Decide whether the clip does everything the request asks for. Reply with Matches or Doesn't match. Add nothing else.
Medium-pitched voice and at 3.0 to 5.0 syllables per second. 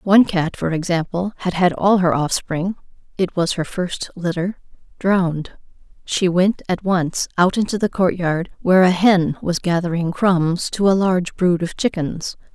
Matches